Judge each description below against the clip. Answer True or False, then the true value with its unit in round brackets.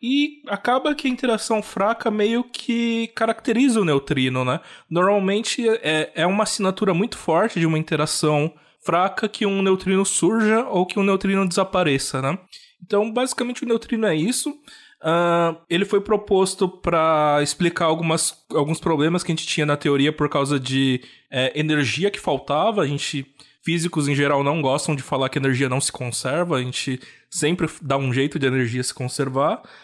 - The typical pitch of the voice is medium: True (170 Hz)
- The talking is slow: False (175 wpm)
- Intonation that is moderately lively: False (6.2 semitones)